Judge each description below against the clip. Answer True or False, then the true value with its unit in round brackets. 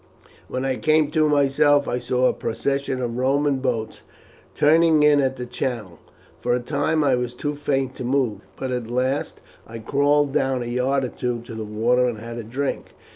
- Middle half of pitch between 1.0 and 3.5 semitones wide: True (2.8 semitones)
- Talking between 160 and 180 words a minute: False (195 wpm)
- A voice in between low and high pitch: False (130 Hz)